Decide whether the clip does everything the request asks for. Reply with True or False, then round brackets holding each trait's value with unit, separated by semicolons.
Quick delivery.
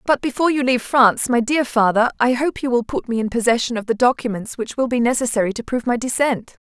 True (245 wpm)